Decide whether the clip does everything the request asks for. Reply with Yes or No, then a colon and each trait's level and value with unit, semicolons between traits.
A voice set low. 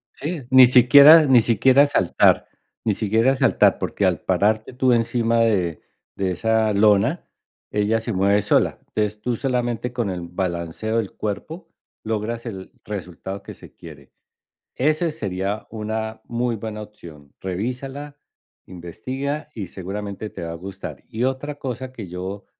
Yes: low, 110 Hz